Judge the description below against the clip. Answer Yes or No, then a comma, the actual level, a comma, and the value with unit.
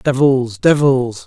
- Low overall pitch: Yes, low, 130 Hz